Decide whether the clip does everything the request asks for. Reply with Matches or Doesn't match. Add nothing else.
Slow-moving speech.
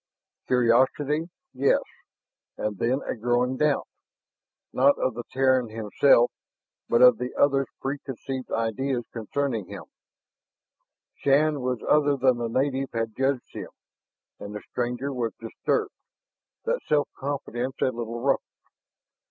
Matches